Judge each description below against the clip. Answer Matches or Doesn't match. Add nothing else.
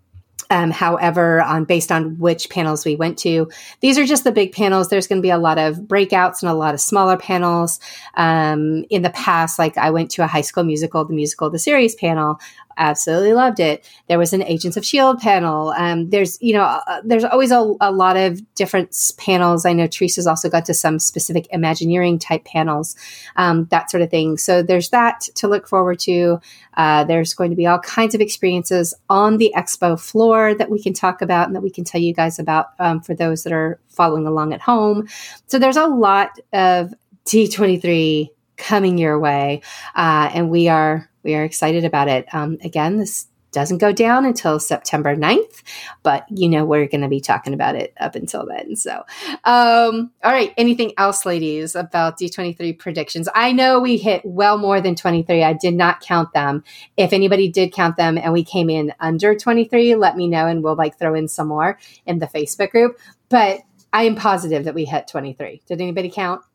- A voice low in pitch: Doesn't match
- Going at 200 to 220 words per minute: Matches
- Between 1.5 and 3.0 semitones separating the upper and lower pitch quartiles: Doesn't match